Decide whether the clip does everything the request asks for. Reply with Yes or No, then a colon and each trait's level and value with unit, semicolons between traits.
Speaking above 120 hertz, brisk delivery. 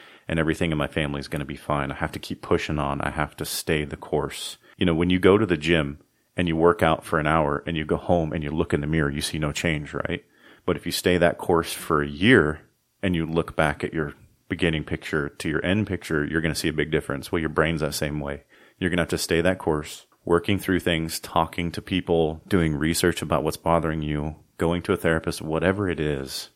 No: very low, 80 Hz; fast, 255 wpm